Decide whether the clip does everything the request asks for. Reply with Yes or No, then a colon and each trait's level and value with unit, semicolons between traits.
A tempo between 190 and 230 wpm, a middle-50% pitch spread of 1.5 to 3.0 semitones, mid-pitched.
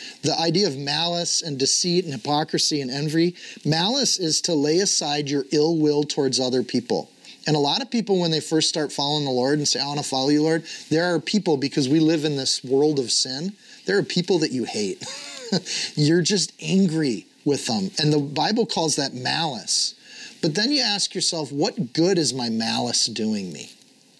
No: average, 200 wpm; average, 3.7 semitones; medium, 155 Hz